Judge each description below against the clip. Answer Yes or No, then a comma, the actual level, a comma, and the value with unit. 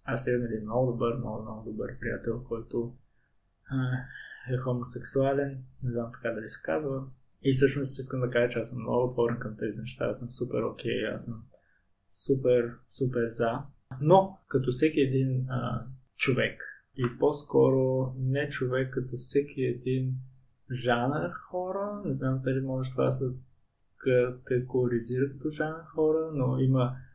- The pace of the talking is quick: No, average, 155 wpm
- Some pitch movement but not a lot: No, narrow, 1.9 semitones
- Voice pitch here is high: No, low, 125 Hz